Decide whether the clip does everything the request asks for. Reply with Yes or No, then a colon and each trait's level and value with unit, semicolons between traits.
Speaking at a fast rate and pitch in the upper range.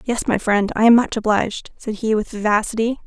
Yes: fast, 215 wpm; high, 220 Hz